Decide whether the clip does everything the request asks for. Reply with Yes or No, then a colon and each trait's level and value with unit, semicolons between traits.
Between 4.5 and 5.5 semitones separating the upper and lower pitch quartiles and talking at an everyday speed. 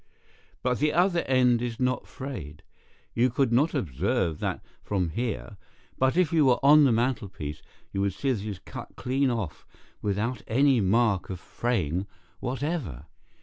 Yes: average, 5.2 semitones; average, 160 wpm